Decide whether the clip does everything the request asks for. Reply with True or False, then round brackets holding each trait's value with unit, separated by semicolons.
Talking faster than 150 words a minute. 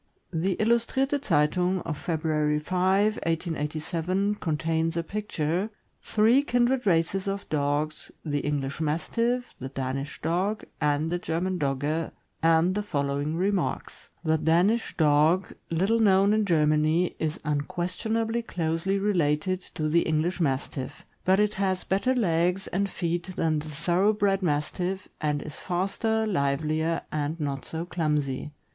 False (135 wpm)